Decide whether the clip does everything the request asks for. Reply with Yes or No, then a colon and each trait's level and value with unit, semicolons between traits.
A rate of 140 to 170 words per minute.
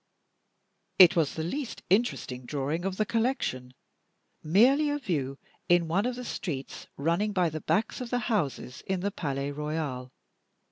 Yes: average, 155 wpm